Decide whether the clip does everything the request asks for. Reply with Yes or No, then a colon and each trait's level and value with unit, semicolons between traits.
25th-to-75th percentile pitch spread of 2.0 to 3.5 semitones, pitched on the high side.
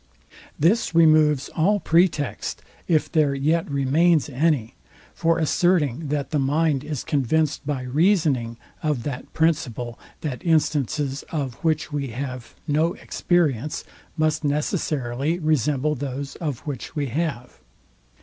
No: average, 3.0 semitones; medium, 150 Hz